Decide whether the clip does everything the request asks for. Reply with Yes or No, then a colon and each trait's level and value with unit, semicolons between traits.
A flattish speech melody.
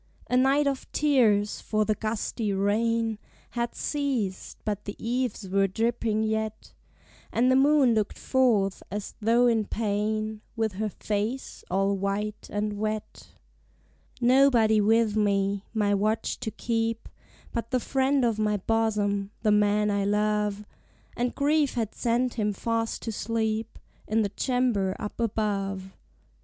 Yes: narrow, 2.2 semitones